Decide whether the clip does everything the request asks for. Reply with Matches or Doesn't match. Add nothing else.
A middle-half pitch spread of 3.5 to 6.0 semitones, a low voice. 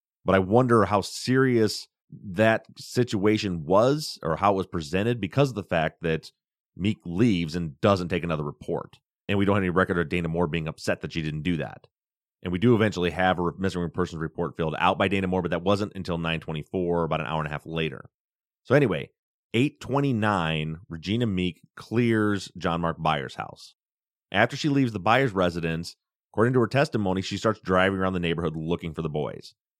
Matches